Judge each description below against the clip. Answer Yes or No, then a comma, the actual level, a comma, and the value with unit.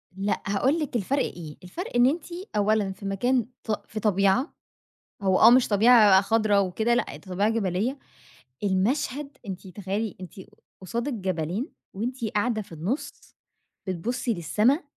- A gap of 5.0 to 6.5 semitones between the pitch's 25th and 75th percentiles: No, average, 4.3 semitones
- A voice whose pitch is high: Yes, high, 210 Hz